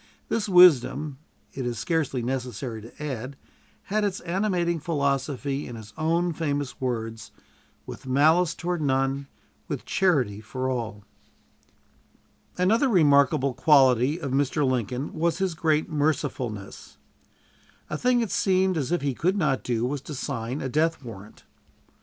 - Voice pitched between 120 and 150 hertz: Yes, medium, 140 Hz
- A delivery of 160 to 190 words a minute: No, average, 140 wpm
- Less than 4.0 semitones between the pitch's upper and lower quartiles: No, average, 4.8 semitones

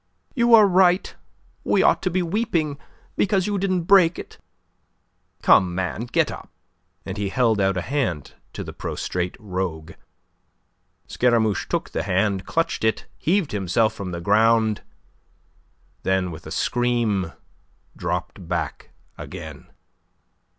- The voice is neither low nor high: No, low, 110 Hz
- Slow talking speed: Yes, slow, 130 wpm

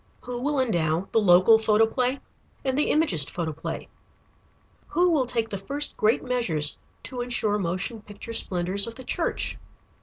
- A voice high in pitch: Yes, high, 225 Hz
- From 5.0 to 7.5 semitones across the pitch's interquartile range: Yes, wide, 5.4 semitones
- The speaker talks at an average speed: Yes, average, 150 wpm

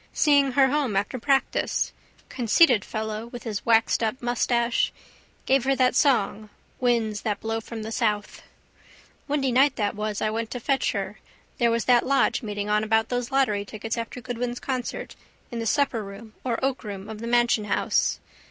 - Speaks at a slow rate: No, average, 170 wpm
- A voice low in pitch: No, high, 235 Hz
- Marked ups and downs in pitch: No, average, 2.9 semitones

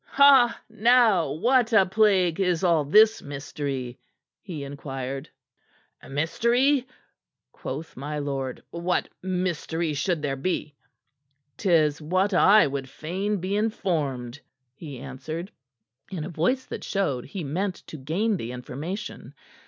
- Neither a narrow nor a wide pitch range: No, wide, 5.8 semitones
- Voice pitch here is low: No, medium, 165 Hz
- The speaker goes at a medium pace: No, slow, 120 wpm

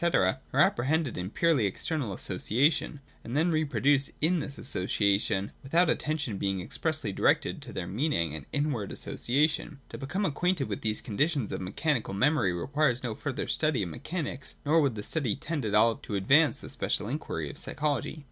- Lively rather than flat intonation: Yes, wide, 6.8 semitones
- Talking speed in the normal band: Yes, average, 175 wpm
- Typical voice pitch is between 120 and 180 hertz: Yes, low, 135 Hz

